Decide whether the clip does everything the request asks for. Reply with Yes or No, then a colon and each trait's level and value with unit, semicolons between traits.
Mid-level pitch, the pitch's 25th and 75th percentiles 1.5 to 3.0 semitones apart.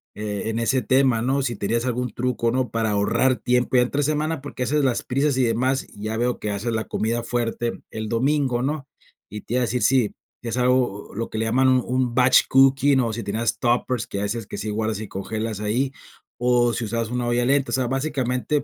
No: low, 120 Hz; narrow, 2.6 semitones